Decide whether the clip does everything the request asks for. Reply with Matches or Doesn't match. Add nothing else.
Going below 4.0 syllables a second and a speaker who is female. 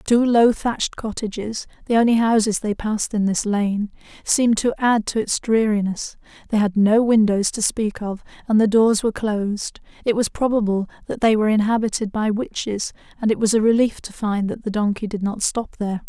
Doesn't match